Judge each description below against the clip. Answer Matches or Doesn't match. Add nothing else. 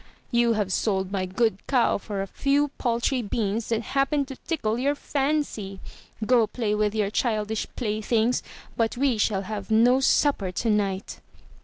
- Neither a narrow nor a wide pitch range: Matches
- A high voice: Matches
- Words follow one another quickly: Doesn't match